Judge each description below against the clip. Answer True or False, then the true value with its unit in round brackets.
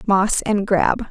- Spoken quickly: False (165 wpm)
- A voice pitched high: True (200 Hz)